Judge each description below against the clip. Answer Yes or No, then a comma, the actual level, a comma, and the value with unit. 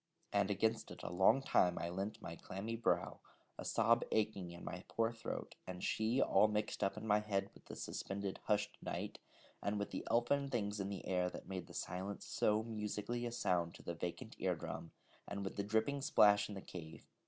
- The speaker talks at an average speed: No, fast, 210 wpm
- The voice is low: Yes, low, 105 Hz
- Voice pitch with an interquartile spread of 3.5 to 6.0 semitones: No, average, 2.7 semitones